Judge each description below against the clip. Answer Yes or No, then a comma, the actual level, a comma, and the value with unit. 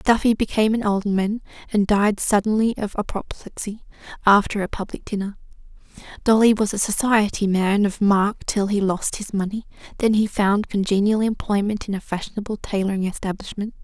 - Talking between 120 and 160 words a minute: Yes, average, 150 wpm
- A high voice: Yes, high, 205 Hz